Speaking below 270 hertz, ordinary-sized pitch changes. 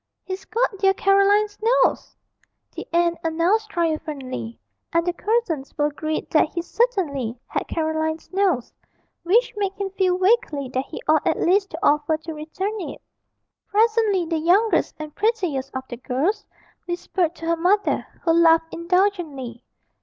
No: very high, 340 Hz; average, 4.4 semitones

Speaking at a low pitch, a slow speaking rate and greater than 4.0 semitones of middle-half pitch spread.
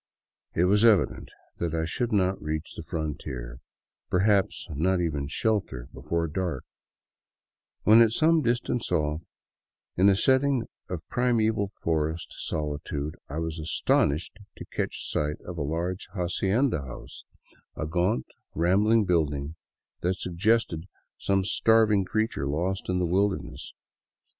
Yes: very low, 90 Hz; slow, 130 wpm; average, 5.1 semitones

